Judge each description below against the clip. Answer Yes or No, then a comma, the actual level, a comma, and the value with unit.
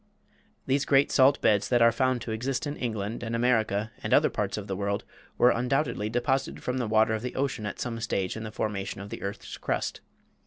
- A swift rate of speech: Yes, fast, 220 wpm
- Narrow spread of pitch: No, average, 3.2 semitones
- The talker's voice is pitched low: Yes, low, 115 Hz